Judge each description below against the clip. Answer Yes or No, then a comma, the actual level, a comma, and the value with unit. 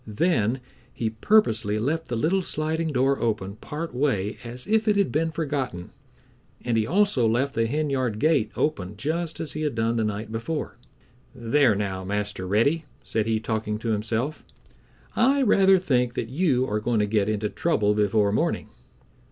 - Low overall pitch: Yes, low, 120 Hz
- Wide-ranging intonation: Yes, wide, 6.4 semitones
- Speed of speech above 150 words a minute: Yes, average, 170 wpm